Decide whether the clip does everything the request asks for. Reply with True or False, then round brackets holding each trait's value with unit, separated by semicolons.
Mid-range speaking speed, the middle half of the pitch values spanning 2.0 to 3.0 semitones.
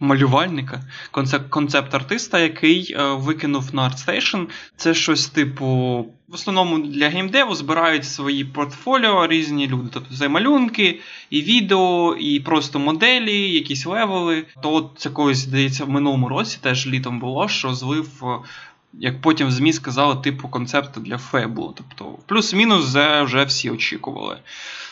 False (135 wpm; 3.9 semitones)